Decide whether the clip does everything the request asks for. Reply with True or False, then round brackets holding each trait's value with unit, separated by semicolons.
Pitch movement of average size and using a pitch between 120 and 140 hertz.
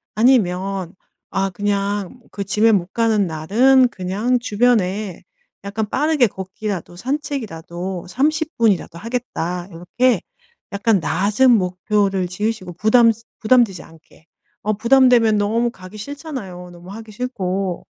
False (4.5 semitones; 205 Hz)